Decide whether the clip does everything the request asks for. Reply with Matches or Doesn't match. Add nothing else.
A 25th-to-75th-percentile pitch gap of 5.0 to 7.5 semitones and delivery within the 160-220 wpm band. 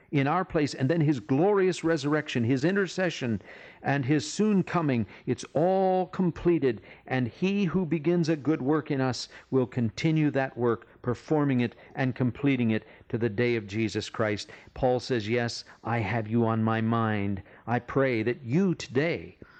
Matches